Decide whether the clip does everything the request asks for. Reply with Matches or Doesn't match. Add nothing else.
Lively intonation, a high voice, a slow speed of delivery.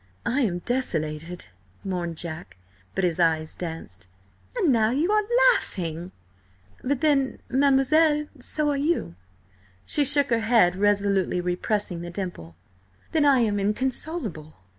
Matches